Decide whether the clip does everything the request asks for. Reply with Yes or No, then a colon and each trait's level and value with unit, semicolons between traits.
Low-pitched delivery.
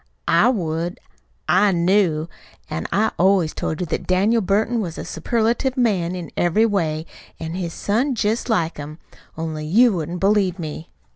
No: medium, 185 Hz